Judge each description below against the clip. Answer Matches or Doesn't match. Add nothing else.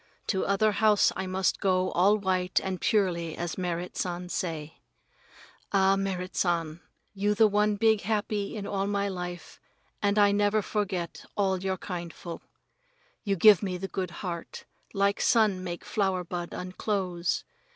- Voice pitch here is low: Doesn't match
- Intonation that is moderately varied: Doesn't match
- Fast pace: Doesn't match